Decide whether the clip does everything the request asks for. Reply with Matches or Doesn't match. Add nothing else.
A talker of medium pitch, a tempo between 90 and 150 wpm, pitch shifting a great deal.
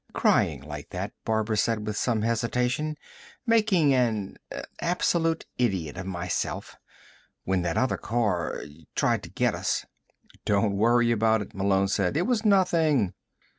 Doesn't match